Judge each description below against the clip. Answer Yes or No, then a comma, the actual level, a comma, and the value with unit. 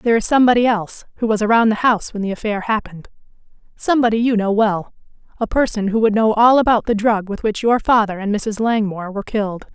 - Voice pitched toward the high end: Yes, high, 215 Hz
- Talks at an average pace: No, fast, 210 wpm